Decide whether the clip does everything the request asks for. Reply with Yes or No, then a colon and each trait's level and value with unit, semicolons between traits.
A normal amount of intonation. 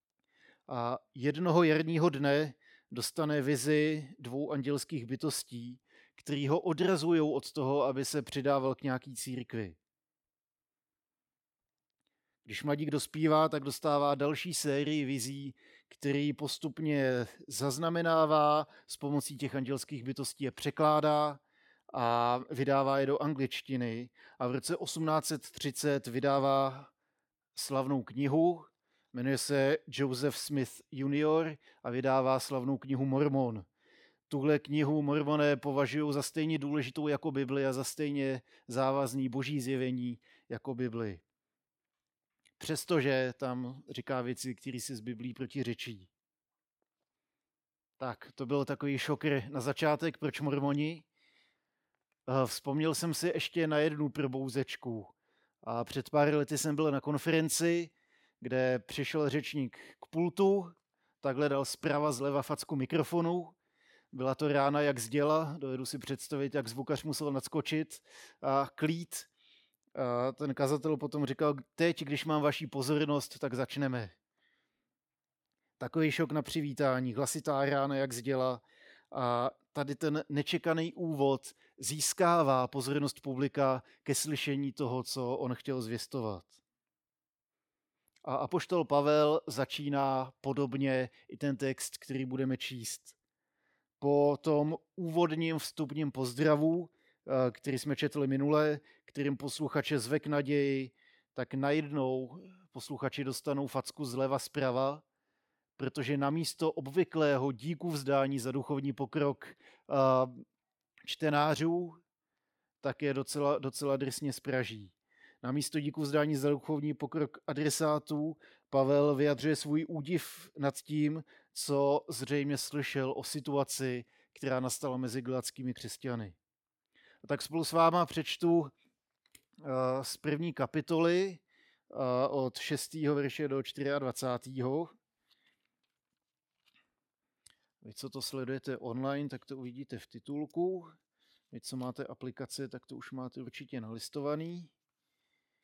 No: narrow, 2.3 semitones